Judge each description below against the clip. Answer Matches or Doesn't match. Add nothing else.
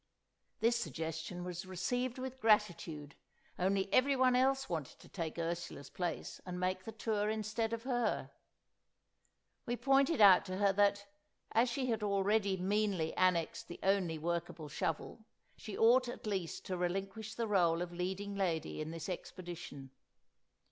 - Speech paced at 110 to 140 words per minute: Doesn't match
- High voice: Matches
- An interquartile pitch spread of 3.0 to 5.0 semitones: Matches